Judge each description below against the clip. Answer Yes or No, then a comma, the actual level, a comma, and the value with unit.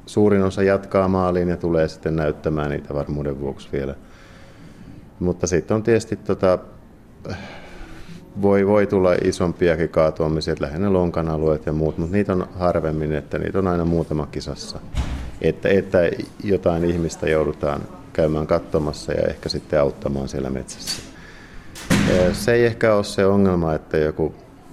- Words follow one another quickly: No, average, 140 wpm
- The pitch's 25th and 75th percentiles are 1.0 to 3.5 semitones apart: No, average, 4.1 semitones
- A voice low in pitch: Yes, very low, 85 Hz